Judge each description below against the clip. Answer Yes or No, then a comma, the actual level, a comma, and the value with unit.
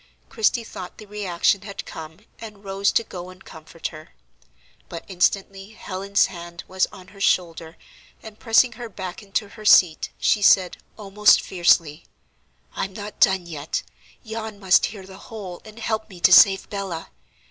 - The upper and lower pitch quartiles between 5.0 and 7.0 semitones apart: No, average, 2.9 semitones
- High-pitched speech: Yes, high, 195 Hz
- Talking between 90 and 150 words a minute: No, average, 160 wpm